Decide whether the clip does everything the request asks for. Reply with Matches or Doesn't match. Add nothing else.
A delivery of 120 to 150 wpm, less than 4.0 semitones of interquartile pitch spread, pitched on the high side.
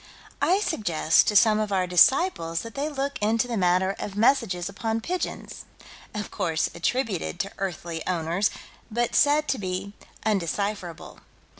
Doesn't match